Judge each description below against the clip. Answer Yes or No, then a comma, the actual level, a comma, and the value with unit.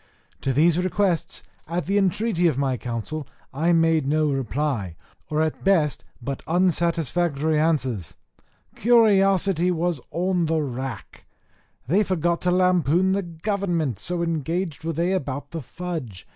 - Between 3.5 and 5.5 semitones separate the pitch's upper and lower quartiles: Yes, average, 3.9 semitones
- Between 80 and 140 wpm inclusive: Yes, slow, 135 wpm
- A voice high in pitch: No, medium, 165 Hz